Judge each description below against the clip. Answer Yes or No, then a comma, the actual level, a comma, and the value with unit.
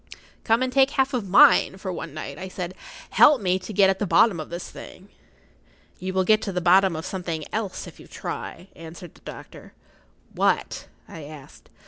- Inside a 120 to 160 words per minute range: No, fast, 205 wpm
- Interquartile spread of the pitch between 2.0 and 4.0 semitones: Yes, average, 3.5 semitones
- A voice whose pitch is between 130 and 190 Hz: Yes, medium, 185 Hz